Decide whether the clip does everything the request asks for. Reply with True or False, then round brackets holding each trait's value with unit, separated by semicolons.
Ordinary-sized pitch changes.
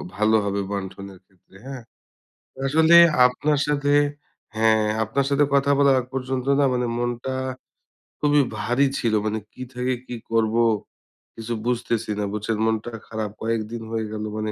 True (3.6 semitones)